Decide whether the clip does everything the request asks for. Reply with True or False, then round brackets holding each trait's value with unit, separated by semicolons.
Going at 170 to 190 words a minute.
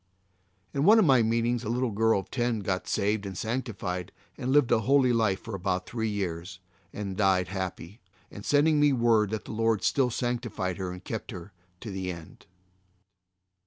True (185 wpm)